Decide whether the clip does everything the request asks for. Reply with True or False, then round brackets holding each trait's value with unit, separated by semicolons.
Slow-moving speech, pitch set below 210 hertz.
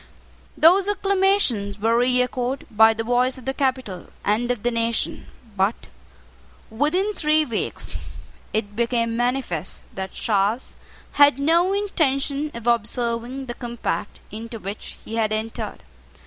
False (130 wpm; 240 Hz)